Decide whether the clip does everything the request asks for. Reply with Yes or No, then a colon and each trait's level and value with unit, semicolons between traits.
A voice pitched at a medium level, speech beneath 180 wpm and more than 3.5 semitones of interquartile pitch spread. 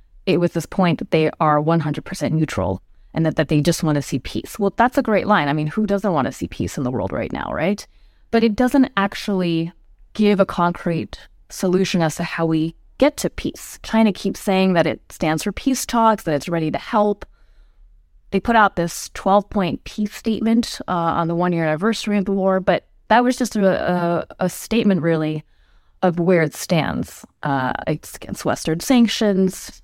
No: medium, 180 Hz; average, 200 wpm; average, 4.6 semitones